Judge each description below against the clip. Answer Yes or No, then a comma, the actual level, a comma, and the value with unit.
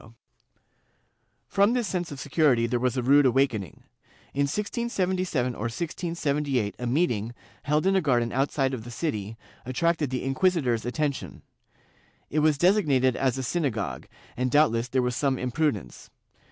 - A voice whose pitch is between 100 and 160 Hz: Yes, low, 135 Hz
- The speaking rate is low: No, average, 155 wpm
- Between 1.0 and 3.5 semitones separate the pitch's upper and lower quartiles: No, average, 4.4 semitones